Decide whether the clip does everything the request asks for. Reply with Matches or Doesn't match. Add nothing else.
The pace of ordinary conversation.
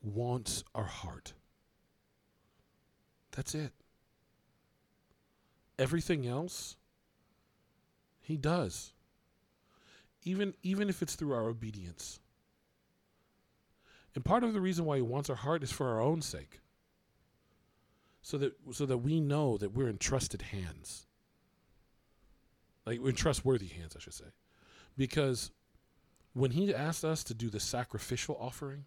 Doesn't match